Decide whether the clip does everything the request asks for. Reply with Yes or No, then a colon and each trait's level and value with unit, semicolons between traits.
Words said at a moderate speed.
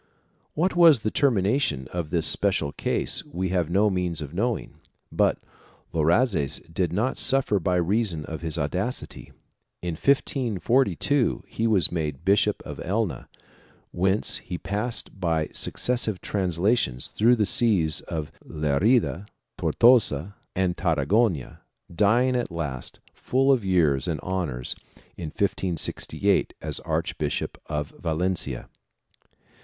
No: slow, 125 wpm